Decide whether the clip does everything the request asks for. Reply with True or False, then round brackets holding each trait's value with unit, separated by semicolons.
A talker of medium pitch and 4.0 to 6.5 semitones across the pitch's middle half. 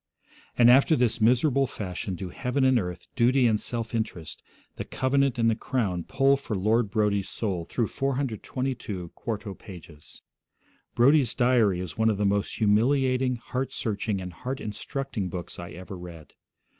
False (115 Hz; 4.9 semitones)